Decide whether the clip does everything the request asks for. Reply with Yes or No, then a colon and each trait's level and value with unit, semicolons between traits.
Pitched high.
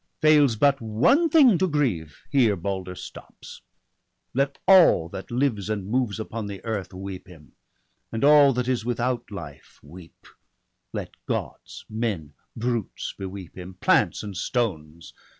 No: low, 110 Hz